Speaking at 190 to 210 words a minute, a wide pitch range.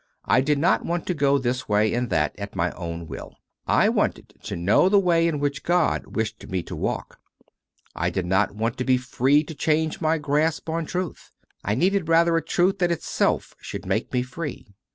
Yes: fast, 205 wpm; wide, 7.6 semitones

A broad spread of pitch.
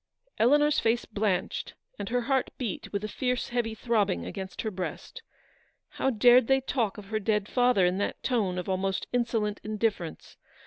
No: average, 3.9 semitones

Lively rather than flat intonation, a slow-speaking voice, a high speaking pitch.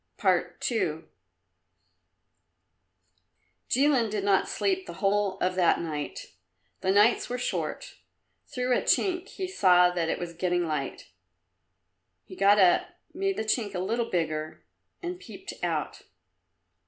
Yes: wide, 6.0 semitones; slow, 130 wpm; high, 200 Hz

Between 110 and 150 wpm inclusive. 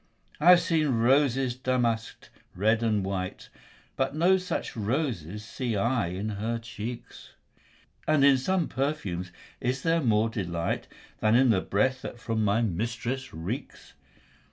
Yes: average, 140 wpm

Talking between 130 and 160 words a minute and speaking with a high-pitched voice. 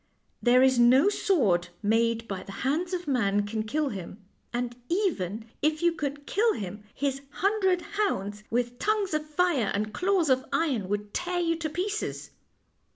No: average, 170 wpm; very high, 270 Hz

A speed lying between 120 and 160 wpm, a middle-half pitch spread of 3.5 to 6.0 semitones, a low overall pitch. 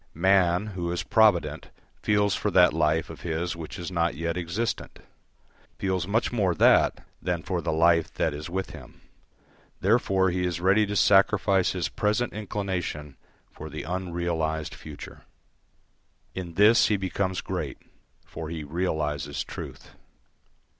No: average, 140 wpm; average, 3.0 semitones; very low, 90 Hz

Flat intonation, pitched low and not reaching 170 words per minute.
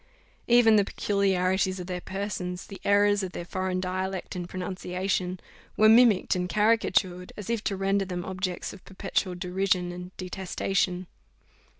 No: narrow, 1.7 semitones; high, 190 Hz; average, 145 wpm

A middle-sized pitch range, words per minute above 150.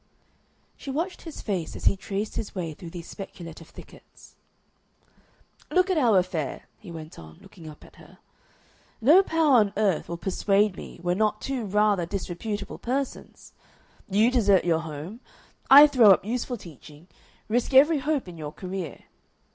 No: wide, 6.4 semitones; average, 160 wpm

